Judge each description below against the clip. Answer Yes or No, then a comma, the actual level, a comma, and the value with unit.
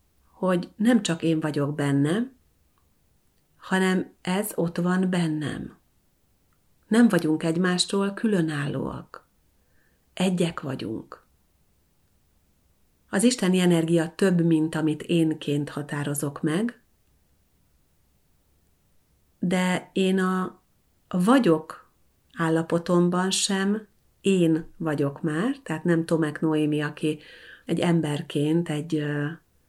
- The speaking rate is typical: No, slow, 85 wpm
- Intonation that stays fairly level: No, average, 4.5 semitones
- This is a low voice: No, medium, 160 Hz